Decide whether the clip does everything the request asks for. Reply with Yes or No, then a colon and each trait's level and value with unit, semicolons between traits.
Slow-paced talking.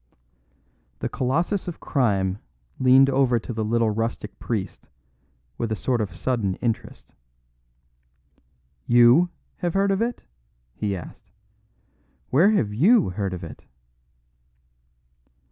Yes: slow, 115 wpm